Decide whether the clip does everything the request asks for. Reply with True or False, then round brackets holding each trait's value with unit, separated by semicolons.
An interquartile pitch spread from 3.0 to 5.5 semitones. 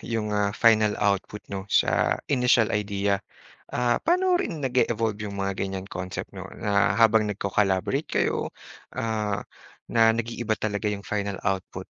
False (2.4 semitones)